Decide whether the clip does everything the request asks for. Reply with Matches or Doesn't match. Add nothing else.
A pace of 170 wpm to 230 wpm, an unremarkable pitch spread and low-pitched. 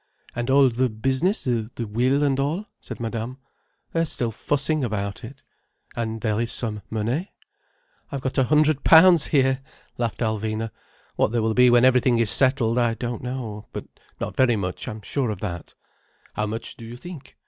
Matches